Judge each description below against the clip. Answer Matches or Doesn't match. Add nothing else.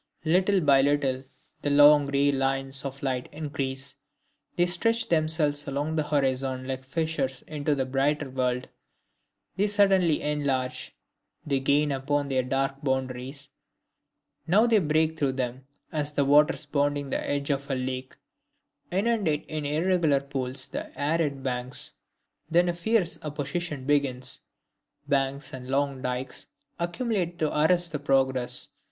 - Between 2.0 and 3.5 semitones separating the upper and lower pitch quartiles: Matches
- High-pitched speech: Doesn't match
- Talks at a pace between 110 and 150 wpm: Matches